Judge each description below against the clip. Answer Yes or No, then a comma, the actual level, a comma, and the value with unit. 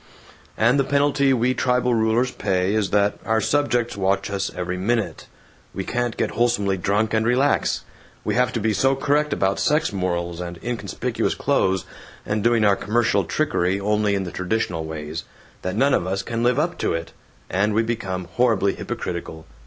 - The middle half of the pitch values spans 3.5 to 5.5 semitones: Yes, average, 4.3 semitones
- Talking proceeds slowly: No, average, 175 wpm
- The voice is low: Yes, low, 110 Hz